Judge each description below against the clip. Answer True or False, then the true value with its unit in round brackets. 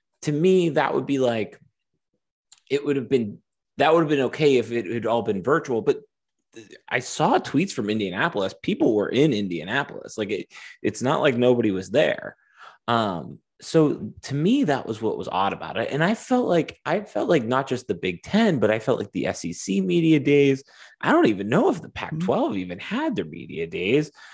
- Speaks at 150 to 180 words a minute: False (205 wpm)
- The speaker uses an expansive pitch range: True (6.1 semitones)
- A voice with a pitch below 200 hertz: True (140 Hz)